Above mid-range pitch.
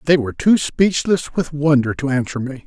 No: medium, 145 Hz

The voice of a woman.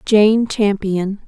Yes: female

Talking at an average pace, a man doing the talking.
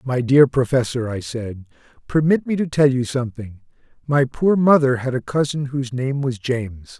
Yes: average, 180 wpm; male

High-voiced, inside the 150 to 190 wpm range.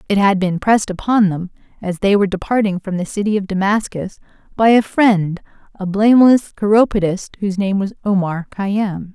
Yes: high, 200 Hz; average, 170 wpm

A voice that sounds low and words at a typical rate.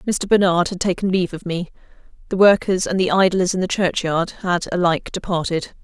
No: medium, 180 Hz; average, 185 wpm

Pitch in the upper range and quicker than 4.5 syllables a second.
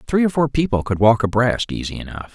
No: low, 120 Hz; 5.9 syllables/s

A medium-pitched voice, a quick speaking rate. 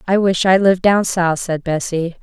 Yes: medium, 180 Hz; fast, 215 wpm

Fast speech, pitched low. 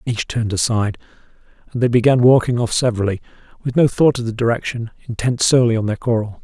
No: average, 185 wpm; low, 115 Hz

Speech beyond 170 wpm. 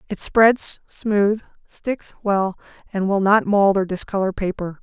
No: average, 150 wpm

